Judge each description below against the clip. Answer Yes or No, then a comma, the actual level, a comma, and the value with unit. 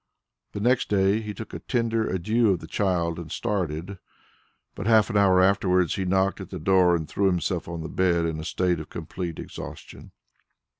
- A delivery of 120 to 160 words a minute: No, average, 195 wpm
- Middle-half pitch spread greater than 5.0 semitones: No, average, 3.2 semitones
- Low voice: Yes, very low, 95 Hz